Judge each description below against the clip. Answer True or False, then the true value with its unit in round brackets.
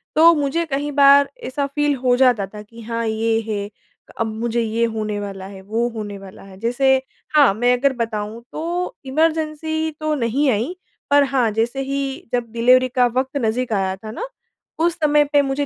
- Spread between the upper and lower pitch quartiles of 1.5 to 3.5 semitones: False (4.4 semitones)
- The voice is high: True (245 Hz)